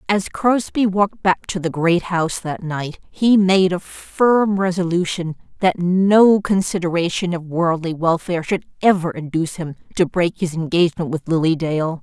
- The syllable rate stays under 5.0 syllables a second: Yes, 4.6 syllables/s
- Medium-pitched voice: Yes, medium, 175 Hz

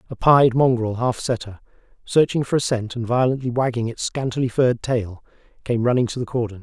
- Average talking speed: Yes, average, 190 wpm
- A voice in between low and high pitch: No, low, 120 Hz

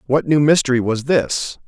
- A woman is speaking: No, male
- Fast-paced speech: No, average, 180 wpm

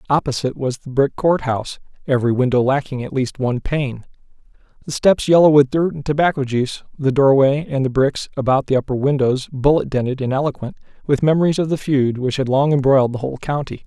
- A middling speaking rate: Yes, average, 195 wpm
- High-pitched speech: No, low, 135 Hz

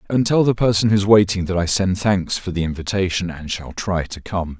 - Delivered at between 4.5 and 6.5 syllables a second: Yes, 5.5 syllables/s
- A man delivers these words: Yes, male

